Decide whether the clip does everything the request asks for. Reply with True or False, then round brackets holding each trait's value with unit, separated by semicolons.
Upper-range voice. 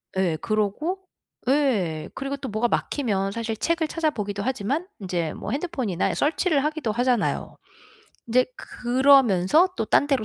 True (245 Hz)